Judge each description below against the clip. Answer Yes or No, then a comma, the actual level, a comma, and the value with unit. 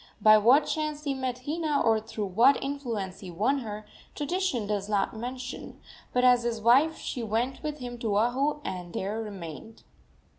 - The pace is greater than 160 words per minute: Yes, average, 175 wpm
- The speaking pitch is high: Yes, high, 240 Hz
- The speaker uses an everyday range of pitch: Yes, average, 4.5 semitones